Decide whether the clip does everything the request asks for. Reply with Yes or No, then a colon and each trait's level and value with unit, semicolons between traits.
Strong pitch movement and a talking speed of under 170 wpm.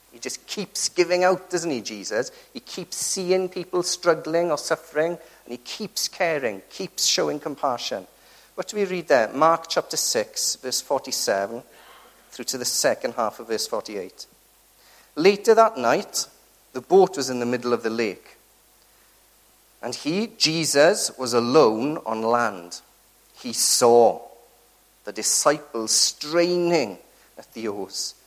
Yes: wide, 7.2 semitones; average, 140 wpm